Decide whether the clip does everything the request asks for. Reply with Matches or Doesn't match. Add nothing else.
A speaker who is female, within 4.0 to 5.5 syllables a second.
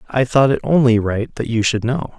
Doesn't match